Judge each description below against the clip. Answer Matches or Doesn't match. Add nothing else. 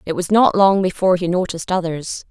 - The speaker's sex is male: Doesn't match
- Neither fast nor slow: Doesn't match